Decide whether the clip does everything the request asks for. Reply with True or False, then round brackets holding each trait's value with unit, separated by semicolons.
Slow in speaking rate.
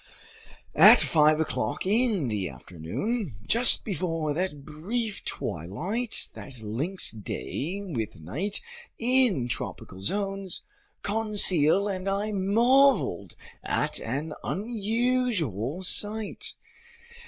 True (95 wpm)